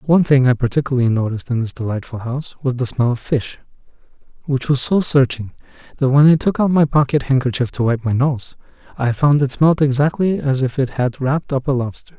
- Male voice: Yes, male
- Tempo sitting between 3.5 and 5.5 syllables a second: No, 5.9 syllables/s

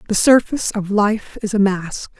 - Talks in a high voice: Yes, high, 205 Hz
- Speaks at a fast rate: No, average, 190 wpm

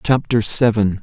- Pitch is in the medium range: No, low, 115 Hz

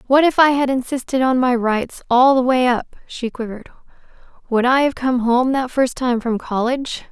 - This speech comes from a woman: Yes, female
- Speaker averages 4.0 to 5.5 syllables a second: Yes, 5.2 syllables/s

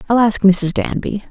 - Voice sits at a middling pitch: No, high, 205 Hz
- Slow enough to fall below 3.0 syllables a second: No, 4.6 syllables/s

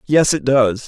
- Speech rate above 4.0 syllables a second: No, 3.9 syllables/s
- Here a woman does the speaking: No, male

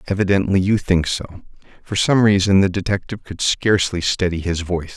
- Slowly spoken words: No, average, 170 wpm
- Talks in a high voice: No, very low, 95 Hz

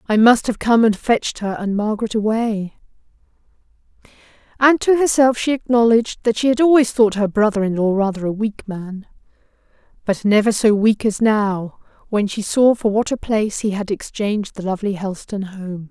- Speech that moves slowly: No, average, 180 wpm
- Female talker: Yes, female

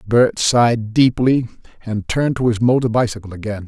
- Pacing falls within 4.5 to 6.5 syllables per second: Yes, 5.3 syllables/s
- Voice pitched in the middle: No, low, 115 Hz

